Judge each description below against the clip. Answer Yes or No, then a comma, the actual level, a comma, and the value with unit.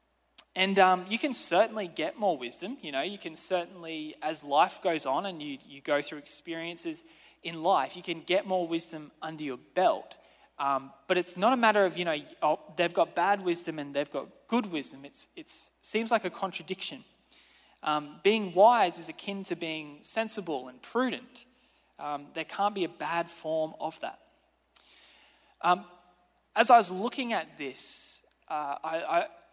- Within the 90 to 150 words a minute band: No, average, 175 wpm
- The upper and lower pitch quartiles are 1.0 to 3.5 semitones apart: No, average, 4.4 semitones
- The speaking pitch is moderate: Yes, medium, 175 Hz